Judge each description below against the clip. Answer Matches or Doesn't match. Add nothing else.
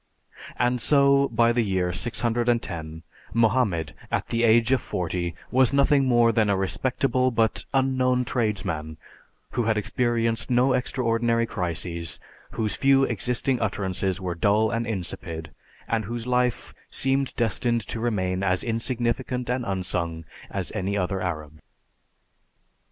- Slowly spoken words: Matches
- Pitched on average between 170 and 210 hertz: Doesn't match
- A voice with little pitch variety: Doesn't match